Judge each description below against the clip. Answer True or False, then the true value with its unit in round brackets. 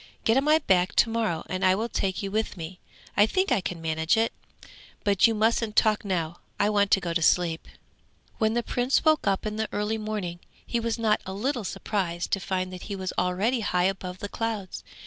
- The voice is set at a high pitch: True (205 Hz)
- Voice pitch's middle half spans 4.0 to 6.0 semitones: False (3.5 semitones)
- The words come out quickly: True (220 wpm)